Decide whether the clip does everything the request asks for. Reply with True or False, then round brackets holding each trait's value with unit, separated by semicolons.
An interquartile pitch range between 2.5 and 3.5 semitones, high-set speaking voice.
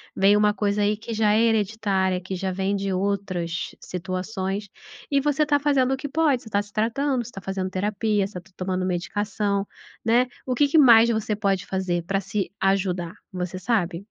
True (3.0 semitones; 200 Hz)